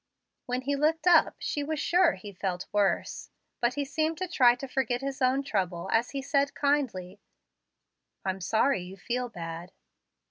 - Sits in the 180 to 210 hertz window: No, very high, 255 Hz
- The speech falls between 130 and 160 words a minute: No, average, 170 wpm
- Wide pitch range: Yes, wide, 6.7 semitones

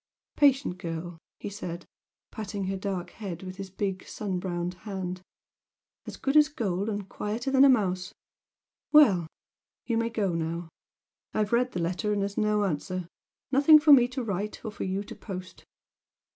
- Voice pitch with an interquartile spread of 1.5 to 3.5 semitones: No, average, 4.0 semitones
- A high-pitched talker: Yes, high, 200 Hz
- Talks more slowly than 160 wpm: No, average, 170 wpm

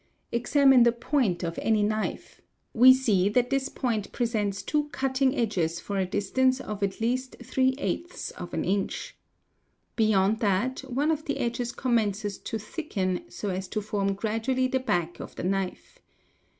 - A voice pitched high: Yes, high, 225 Hz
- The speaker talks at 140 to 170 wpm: Yes, average, 155 wpm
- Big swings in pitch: No, average, 4.6 semitones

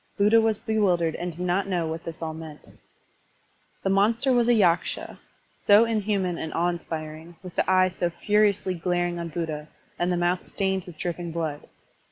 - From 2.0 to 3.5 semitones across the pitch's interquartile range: Yes, average, 3.1 semitones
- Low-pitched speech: No, medium, 175 Hz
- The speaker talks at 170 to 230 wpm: Yes, average, 180 wpm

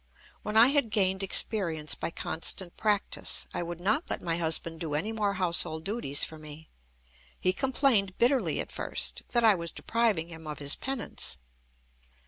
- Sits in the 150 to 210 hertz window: Yes, medium, 185 Hz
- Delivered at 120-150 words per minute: No, average, 165 wpm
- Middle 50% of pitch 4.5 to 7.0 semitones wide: Yes, average, 5.3 semitones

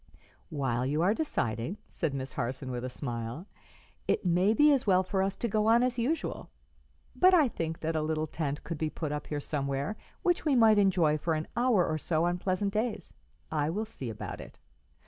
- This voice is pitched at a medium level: Yes, medium, 165 Hz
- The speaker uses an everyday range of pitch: No, wide, 6.7 semitones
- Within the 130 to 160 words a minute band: No, fast, 205 wpm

